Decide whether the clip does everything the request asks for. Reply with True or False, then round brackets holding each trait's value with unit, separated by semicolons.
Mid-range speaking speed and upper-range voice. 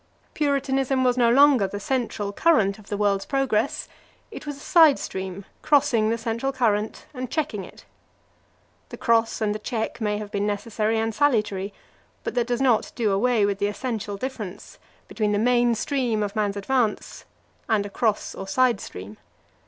True (175 wpm; 225 Hz)